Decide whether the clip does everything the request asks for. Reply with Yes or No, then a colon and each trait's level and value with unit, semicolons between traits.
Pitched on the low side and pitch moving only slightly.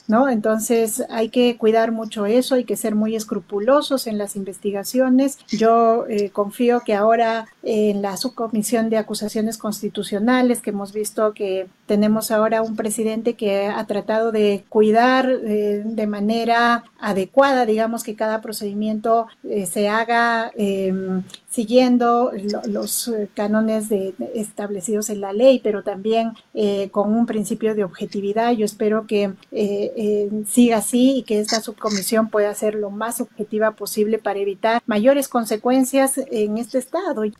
No: high, 220 Hz; narrow, 2.0 semitones